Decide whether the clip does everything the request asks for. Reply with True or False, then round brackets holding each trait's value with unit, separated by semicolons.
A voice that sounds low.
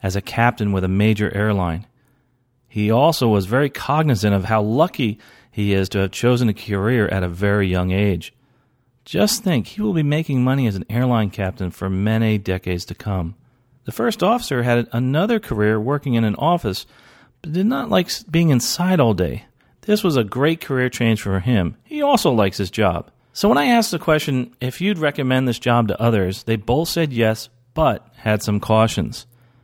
True (120 Hz)